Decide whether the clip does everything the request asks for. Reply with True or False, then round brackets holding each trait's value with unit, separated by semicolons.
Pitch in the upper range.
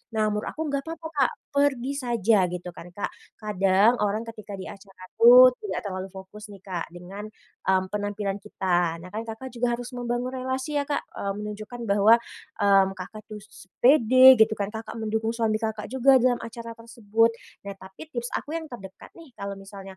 True (220 Hz)